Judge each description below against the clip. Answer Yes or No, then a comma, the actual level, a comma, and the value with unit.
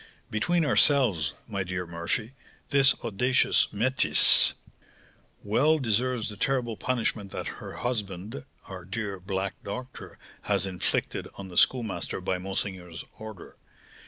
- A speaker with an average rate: No, slow, 120 wpm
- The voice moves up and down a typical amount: Yes, average, 4.8 semitones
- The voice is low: Yes, low, 105 Hz